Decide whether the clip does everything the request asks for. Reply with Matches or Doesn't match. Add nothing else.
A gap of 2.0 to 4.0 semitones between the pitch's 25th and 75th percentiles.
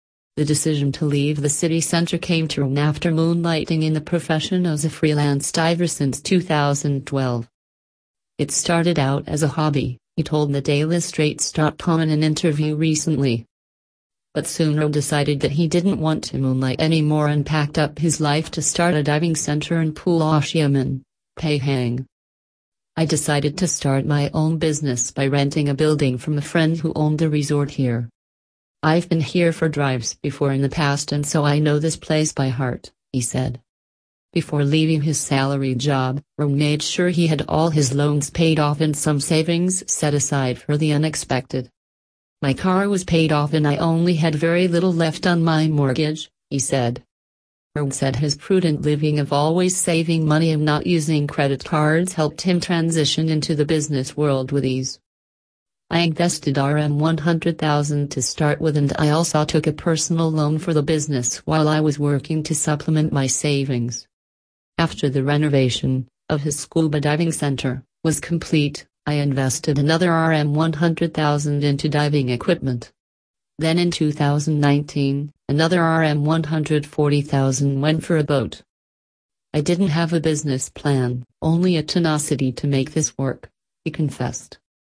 Matches